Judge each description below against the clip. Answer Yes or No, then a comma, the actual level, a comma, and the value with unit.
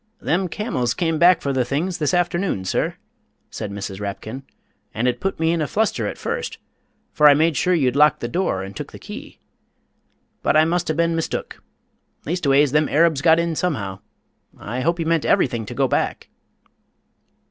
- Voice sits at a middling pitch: Yes, medium, 155 Hz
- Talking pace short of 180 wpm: No, average, 185 wpm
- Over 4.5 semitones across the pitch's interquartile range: Yes, average, 5.2 semitones